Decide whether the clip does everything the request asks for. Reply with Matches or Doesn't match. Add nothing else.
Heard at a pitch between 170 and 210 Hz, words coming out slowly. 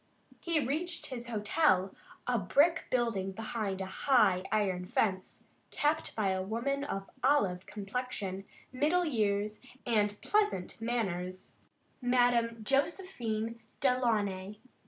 Doesn't match